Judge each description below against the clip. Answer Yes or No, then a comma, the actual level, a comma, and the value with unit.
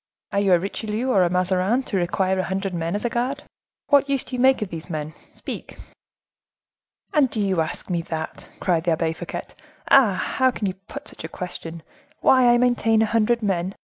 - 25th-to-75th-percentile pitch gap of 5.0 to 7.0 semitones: Yes, wide, 5.6 semitones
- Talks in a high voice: Yes, high, 195 Hz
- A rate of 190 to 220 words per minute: Yes, average, 200 wpm